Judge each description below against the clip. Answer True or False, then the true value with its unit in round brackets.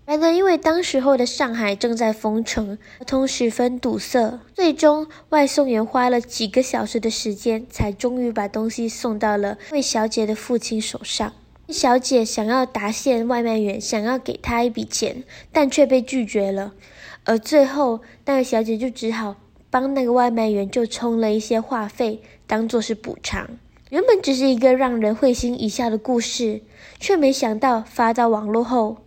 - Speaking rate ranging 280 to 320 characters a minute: False (260 characters per minute)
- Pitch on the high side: True (240 Hz)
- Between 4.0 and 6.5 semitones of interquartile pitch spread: False (2.9 semitones)